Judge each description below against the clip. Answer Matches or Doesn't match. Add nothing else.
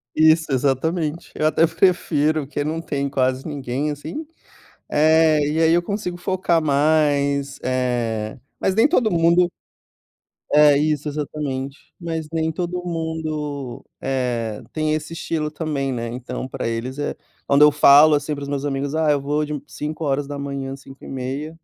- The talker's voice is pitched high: Doesn't match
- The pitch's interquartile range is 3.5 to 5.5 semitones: Doesn't match